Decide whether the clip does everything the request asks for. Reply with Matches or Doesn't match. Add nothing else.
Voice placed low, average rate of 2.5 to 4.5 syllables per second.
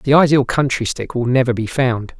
Doesn't match